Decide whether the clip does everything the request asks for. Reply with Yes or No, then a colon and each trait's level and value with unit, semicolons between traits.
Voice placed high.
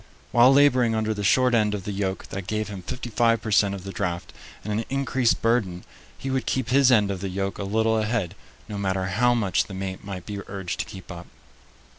No: low, 105 Hz